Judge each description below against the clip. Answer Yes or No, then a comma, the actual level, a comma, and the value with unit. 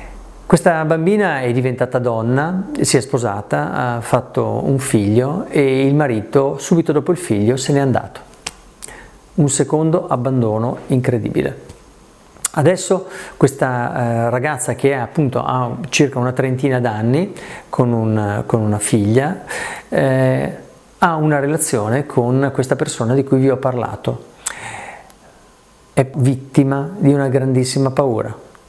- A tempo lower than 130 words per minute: Yes, average, 120 wpm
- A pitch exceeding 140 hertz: No, low, 135 Hz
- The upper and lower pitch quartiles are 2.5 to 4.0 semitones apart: Yes, average, 3.2 semitones